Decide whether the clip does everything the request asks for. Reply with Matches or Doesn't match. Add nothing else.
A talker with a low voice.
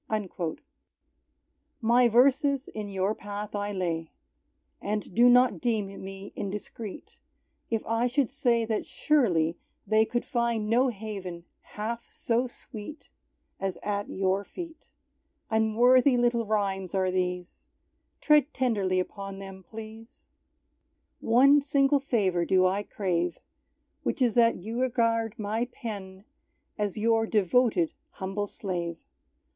Doesn't match